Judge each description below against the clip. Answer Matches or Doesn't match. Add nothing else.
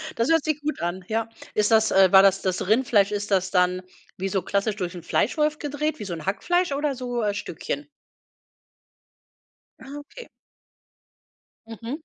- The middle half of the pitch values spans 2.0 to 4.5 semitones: Doesn't match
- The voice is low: Doesn't match